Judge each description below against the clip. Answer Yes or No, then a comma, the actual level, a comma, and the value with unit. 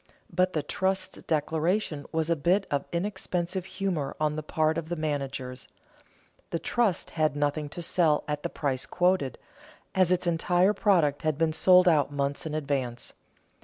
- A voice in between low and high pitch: Yes, medium, 160 Hz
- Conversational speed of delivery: Yes, average, 165 wpm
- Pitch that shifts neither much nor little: Yes, average, 3.8 semitones